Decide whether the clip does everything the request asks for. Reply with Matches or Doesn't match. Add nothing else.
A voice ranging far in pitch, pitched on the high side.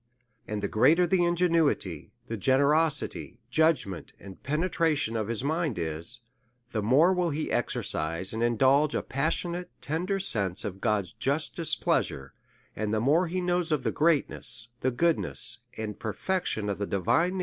Doesn't match